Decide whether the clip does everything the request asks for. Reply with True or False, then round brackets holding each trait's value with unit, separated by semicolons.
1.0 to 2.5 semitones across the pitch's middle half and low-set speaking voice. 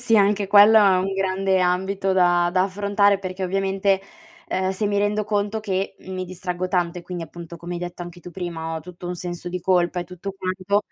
False (2.0 semitones; 185 Hz)